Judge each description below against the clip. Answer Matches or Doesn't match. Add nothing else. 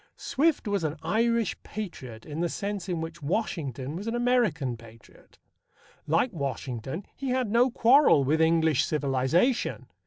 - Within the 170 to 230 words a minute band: Doesn't match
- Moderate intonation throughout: Doesn't match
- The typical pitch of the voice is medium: Matches